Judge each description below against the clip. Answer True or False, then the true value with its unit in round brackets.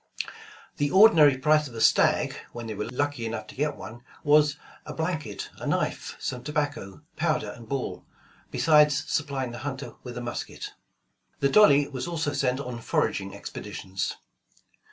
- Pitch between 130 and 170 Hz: True (140 Hz)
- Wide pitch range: False (3.7 semitones)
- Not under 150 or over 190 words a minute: True (160 wpm)